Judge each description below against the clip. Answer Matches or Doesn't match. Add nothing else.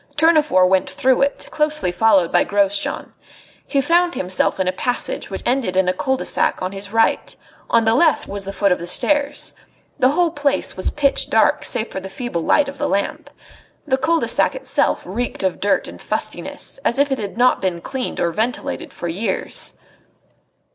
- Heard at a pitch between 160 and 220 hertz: Doesn't match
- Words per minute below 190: Doesn't match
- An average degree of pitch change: Doesn't match